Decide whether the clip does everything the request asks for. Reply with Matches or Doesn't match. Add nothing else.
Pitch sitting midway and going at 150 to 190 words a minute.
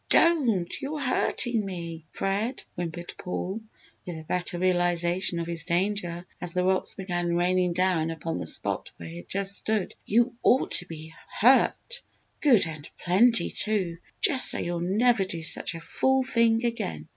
Matches